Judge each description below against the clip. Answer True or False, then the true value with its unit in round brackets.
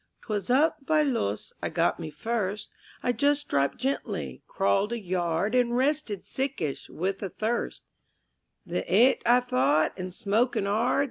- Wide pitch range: True (5.7 semitones)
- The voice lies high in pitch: True (215 Hz)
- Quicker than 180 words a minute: False (155 wpm)